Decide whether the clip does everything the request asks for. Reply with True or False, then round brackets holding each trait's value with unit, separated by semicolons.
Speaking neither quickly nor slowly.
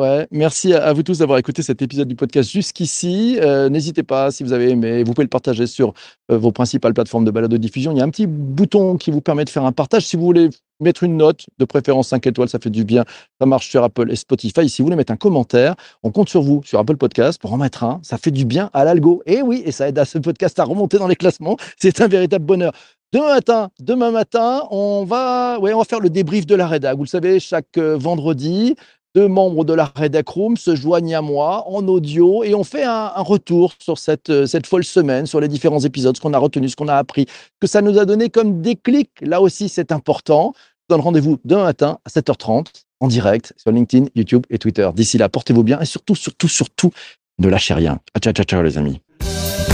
False (245 wpm)